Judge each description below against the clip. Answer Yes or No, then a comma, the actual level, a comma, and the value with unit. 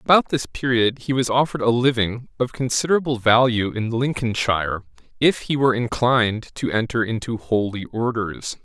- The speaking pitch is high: No, low, 120 Hz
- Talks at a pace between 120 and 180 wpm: Yes, average, 155 wpm